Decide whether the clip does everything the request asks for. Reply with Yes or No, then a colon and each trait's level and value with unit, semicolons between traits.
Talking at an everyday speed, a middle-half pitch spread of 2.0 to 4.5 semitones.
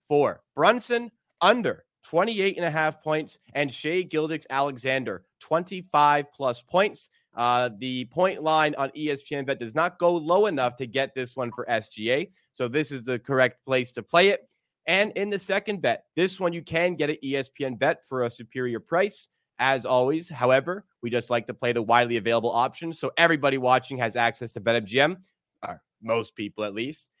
No: average, 185 wpm; average, 5.2 semitones